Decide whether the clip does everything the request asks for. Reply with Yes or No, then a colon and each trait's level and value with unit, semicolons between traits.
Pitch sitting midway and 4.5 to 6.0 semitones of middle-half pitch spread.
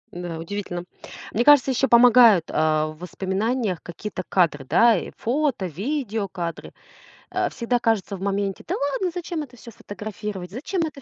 No: high, 210 Hz; wide, 5.6 semitones